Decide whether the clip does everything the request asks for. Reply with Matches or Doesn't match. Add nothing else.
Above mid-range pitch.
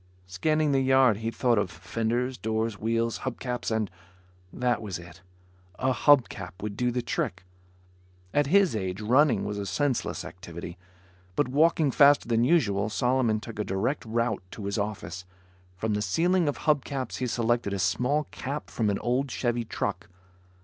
Doesn't match